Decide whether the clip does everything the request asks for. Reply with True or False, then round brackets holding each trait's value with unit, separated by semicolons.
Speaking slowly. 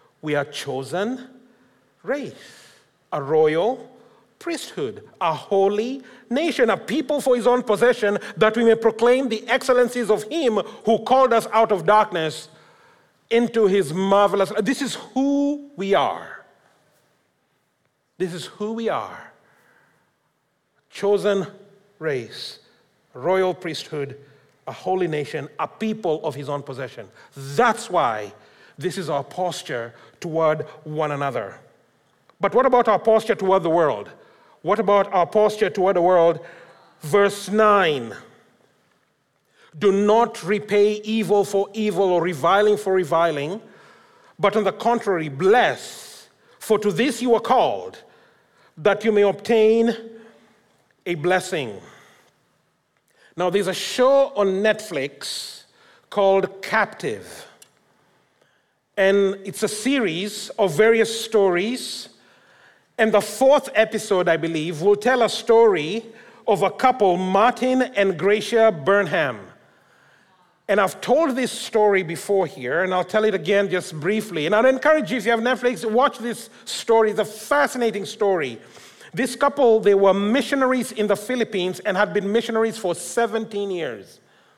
True (130 wpm)